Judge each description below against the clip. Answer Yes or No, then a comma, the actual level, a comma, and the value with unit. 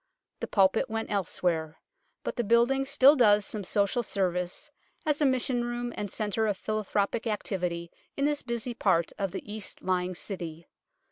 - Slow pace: No, average, 160 wpm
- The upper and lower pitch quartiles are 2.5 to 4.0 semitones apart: No, average, 4.5 semitones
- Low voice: No, high, 210 Hz